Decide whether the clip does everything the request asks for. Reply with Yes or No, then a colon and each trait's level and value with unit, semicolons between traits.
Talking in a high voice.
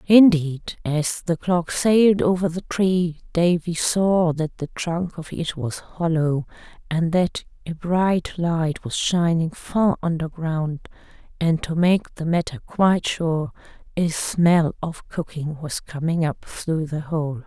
No: medium, 165 Hz